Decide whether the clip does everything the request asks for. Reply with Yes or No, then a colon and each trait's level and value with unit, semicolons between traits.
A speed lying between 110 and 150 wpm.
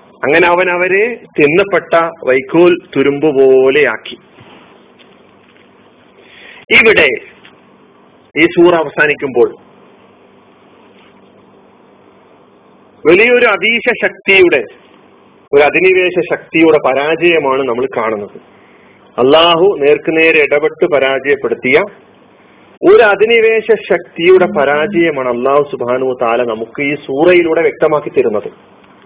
No: average, 70 wpm